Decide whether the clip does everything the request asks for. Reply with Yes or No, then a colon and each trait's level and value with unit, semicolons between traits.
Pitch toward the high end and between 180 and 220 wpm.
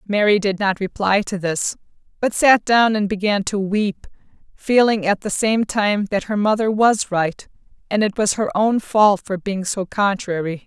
Yes: high, 205 Hz; average, 185 wpm